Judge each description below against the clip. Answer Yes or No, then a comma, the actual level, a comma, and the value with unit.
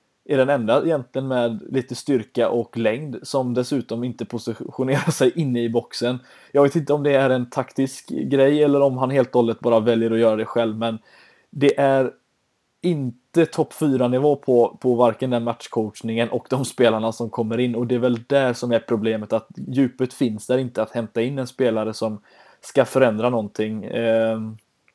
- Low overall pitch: Yes, low, 125 Hz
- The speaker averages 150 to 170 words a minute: No, average, 190 wpm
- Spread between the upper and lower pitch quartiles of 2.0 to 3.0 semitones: Yes, narrow, 2.5 semitones